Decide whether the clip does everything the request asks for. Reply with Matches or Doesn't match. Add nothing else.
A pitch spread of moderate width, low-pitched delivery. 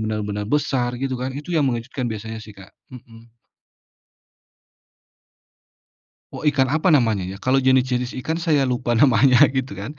Matches